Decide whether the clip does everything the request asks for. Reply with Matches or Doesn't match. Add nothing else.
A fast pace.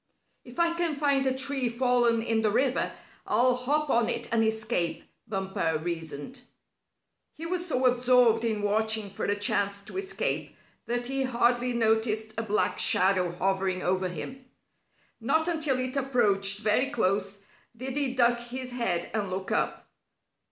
Doesn't match